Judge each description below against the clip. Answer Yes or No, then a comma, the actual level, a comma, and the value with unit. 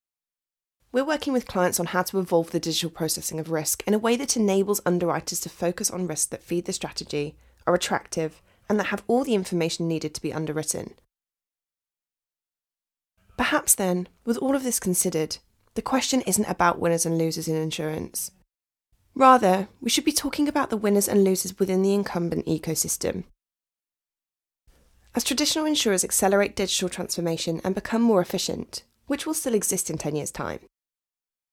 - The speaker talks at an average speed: Yes, average, 165 wpm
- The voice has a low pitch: No, medium, 185 Hz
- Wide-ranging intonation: No, average, 5.0 semitones